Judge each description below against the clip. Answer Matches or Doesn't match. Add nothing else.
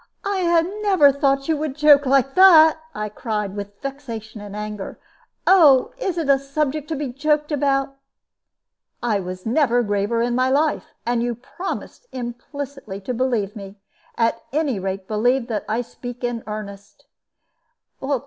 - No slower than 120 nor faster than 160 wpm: Matches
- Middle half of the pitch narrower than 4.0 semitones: Doesn't match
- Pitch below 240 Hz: Doesn't match